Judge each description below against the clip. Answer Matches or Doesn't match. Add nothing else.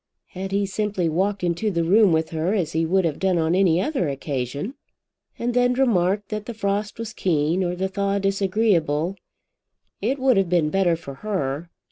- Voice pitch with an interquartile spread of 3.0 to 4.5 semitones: Matches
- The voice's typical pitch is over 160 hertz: Matches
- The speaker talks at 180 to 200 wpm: Matches